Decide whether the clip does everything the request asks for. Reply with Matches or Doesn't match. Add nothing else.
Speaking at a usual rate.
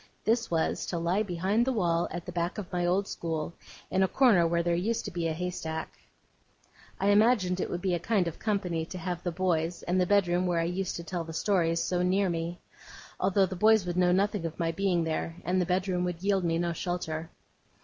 Doesn't match